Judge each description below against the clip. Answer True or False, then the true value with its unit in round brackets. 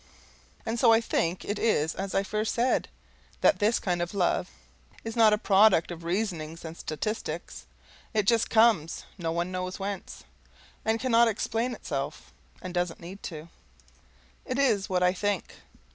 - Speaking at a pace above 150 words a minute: True (160 wpm)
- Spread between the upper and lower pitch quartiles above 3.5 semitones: True (4.5 semitones)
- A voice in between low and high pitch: False (195 Hz)